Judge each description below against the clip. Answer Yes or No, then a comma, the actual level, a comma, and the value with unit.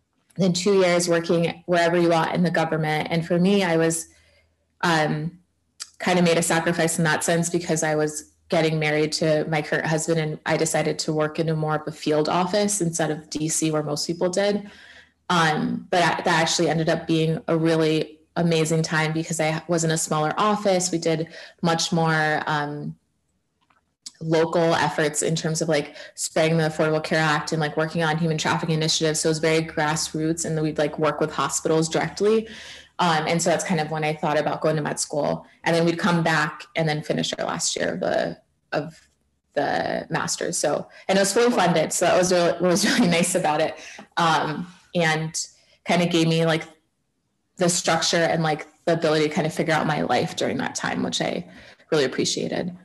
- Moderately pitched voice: Yes, medium, 160 Hz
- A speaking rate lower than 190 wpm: No, average, 200 wpm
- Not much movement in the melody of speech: Yes, narrow, 1.7 semitones